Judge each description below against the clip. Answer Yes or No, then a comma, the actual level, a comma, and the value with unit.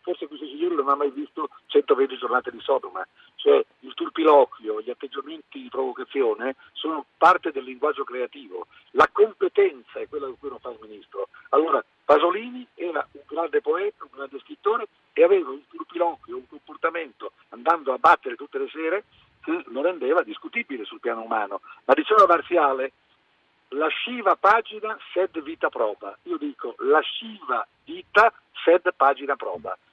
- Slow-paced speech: No, average, 160 wpm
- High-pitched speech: Yes, very high, 370 Hz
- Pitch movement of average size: No, wide, 7.9 semitones